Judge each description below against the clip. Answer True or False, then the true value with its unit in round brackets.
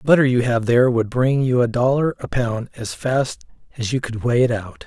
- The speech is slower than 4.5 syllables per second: False (5.3 syllables/s)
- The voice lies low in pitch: True (125 Hz)